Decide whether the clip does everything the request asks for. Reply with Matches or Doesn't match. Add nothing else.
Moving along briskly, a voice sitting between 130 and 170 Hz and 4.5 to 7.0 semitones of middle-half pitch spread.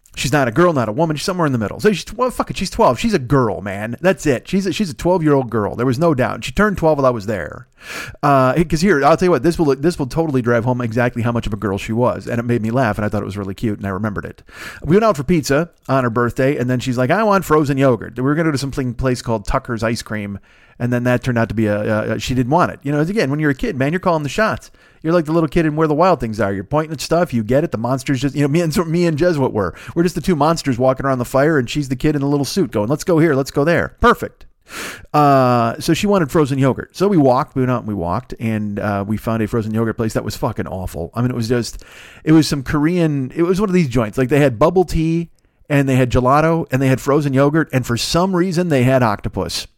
Matches